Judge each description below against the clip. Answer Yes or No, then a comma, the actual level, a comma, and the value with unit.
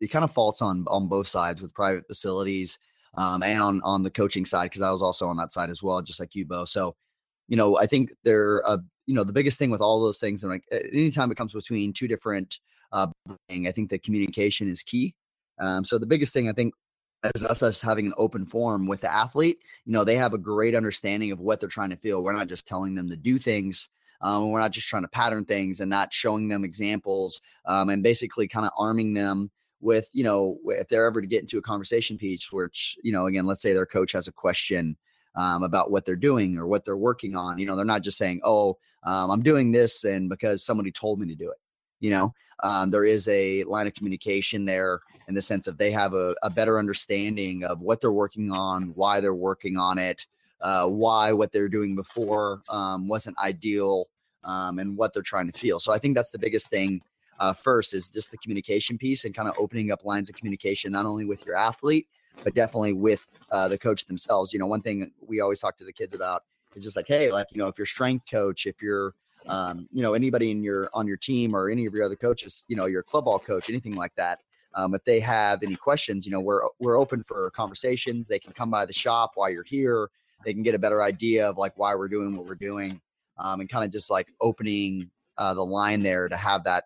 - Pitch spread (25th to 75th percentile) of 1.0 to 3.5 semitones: Yes, narrow, 2.6 semitones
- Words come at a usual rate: No, fast, 245 wpm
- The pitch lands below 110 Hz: Yes, low, 100 Hz